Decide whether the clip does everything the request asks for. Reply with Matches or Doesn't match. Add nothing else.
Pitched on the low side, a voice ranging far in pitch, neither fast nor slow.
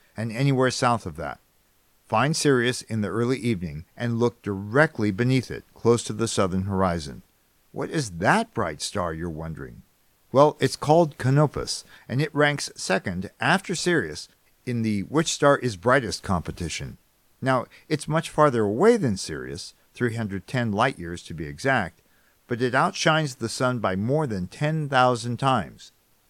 Matches